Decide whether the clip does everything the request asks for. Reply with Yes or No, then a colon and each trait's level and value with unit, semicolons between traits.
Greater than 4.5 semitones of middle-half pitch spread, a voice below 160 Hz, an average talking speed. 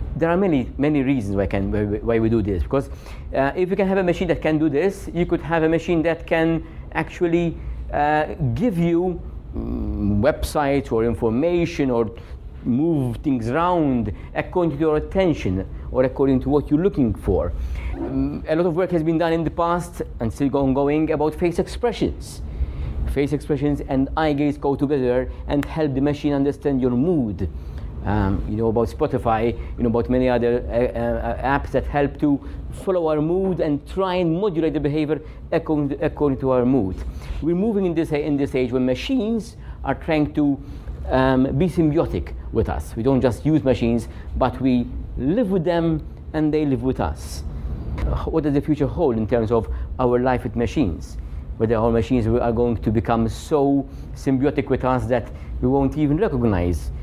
Yes: wide, 5.5 semitones; low, 135 Hz; average, 185 wpm